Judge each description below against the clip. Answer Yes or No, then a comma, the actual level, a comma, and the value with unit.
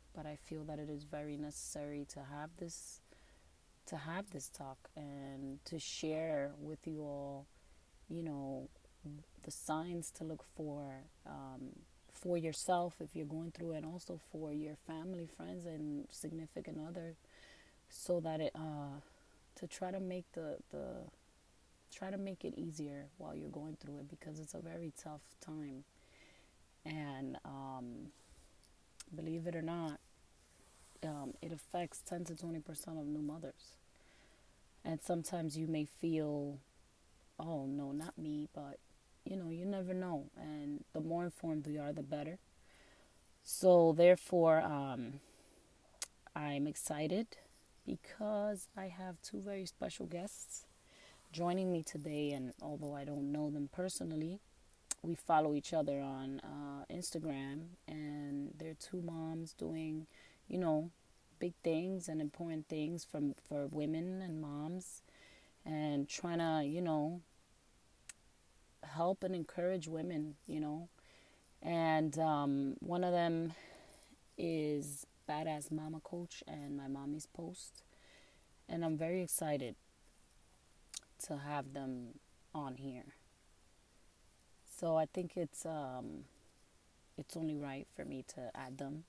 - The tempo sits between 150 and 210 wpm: No, slow, 135 wpm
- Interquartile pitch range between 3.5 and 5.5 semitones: No, narrow, 2.6 semitones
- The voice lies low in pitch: No, medium, 155 Hz